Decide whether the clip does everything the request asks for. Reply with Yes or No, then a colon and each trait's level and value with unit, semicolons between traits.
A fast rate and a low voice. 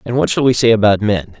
Yes: fast, 300 wpm; low, 110 Hz